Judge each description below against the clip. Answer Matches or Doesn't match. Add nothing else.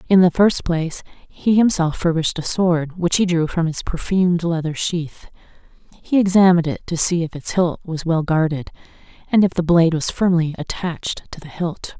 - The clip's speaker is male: Doesn't match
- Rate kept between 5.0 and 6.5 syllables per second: Matches